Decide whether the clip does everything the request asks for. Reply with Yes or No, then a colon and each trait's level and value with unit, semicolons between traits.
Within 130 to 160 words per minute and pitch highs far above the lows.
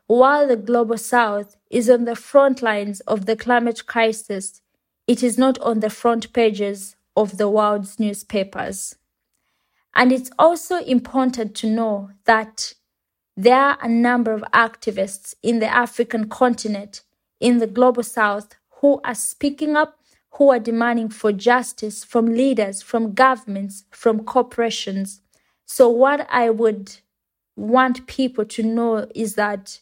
No: average, 140 wpm; average, 2.7 semitones